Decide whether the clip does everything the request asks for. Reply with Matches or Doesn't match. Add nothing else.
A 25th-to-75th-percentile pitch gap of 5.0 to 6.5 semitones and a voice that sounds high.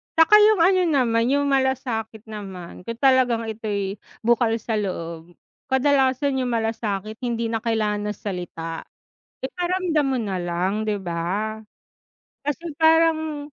Matches